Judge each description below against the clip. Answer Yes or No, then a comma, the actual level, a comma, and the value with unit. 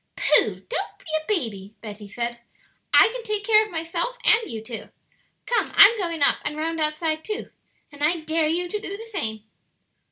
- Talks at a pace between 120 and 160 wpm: No, average, 190 wpm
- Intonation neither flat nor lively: No, wide, 6.0 semitones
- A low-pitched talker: No, very high, 330 Hz